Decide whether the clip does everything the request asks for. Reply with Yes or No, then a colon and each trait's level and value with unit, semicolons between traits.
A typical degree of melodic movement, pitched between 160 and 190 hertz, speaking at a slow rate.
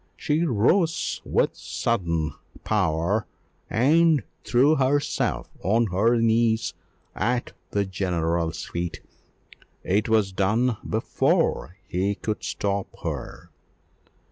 No: average, 4.7 semitones; low, 105 Hz; slow, 95 wpm